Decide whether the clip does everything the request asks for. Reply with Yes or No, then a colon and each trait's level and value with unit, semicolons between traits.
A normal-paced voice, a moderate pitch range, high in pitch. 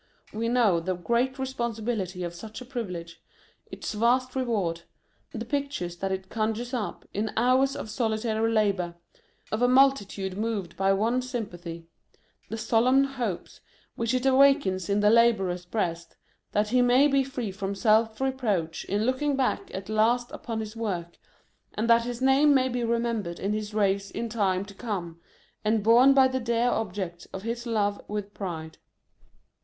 Yes: average, 165 wpm; average, 4.1 semitones; high, 220 Hz